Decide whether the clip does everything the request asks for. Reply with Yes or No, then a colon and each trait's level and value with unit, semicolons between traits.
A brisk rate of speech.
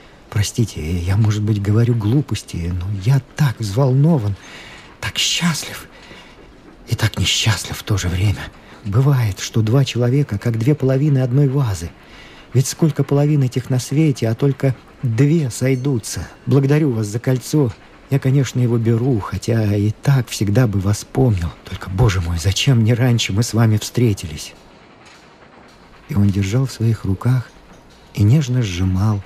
No: average, 150 wpm